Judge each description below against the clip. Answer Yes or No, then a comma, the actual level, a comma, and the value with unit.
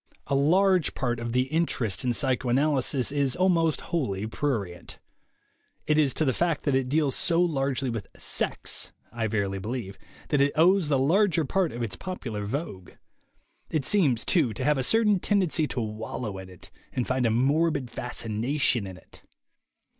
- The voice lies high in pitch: No, low, 135 Hz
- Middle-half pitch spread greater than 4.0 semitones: Yes, average, 5.3 semitones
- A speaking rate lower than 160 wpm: No, average, 170 wpm